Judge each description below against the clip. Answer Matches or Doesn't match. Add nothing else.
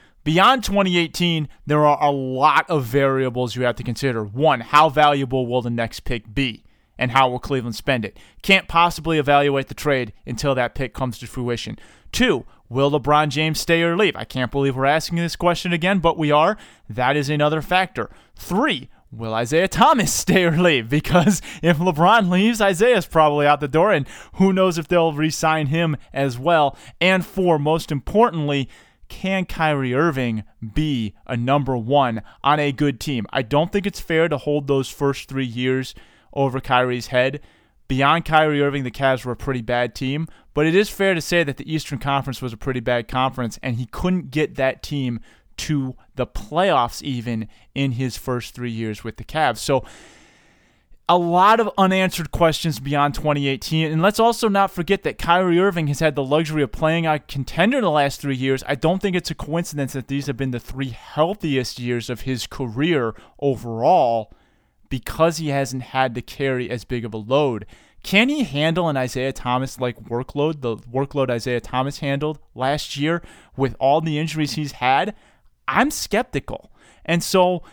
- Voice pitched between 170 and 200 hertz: Doesn't match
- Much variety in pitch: Doesn't match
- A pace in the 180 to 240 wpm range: Matches